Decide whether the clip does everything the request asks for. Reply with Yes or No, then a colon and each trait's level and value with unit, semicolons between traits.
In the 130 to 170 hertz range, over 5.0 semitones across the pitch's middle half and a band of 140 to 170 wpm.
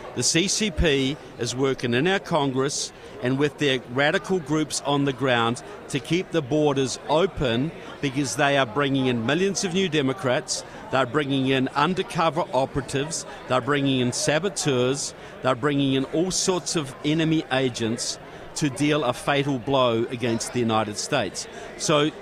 No: medium, 140 Hz; average, 3.2 semitones; average, 150 wpm